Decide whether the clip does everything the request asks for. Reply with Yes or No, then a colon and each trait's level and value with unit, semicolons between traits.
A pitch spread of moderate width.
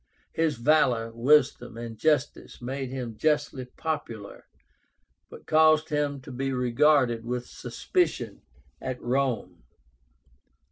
Yes: average, 3.8 semitones